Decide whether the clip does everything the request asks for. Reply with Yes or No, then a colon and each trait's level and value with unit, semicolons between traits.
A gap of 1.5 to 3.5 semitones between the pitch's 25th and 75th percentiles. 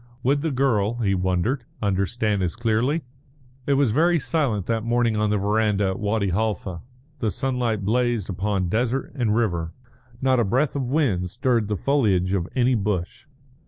No: average, 4.2 semitones